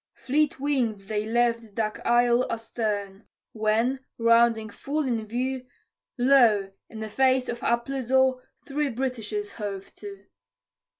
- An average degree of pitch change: Yes, average, 3.3 semitones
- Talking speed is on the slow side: Yes, slow, 120 wpm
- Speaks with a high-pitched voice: Yes, high, 235 Hz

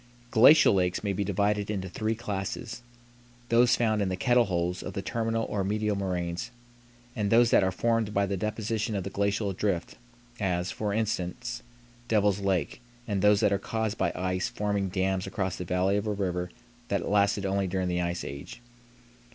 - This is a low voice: Yes, low, 100 Hz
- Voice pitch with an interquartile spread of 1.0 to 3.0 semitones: Yes, narrow, 2.5 semitones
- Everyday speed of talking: Yes, average, 185 wpm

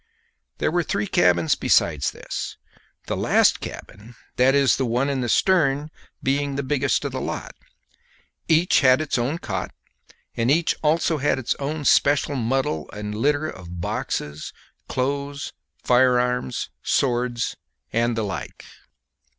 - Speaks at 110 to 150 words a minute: Yes, slow, 135 wpm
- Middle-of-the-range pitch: No, low, 130 Hz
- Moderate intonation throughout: Yes, average, 3.7 semitones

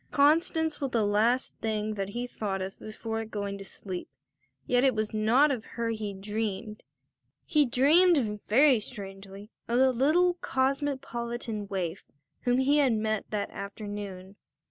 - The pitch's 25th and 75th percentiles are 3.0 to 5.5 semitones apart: Yes, average, 4.3 semitones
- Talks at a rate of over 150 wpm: No, average, 145 wpm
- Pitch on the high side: Yes, high, 225 Hz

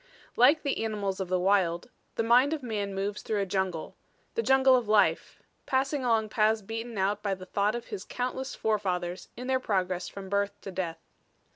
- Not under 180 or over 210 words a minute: Yes, average, 190 wpm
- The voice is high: Yes, high, 210 Hz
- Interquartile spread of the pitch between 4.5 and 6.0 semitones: No, average, 4.1 semitones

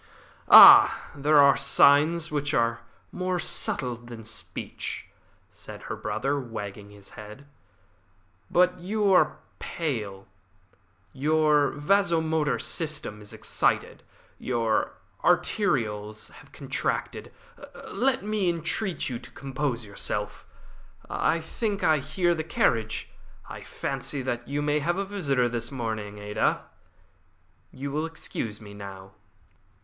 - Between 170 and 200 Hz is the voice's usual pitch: No, medium, 140 Hz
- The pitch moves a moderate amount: No, wide, 6.4 semitones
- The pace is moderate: No, slow, 115 wpm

